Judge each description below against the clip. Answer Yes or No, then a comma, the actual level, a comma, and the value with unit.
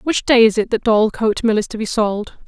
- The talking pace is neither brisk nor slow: No, fast, 265 wpm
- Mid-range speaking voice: No, high, 220 Hz